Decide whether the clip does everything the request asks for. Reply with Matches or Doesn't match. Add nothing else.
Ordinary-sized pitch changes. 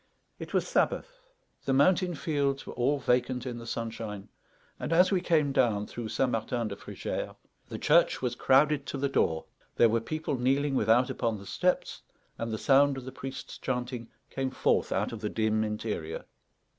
Matches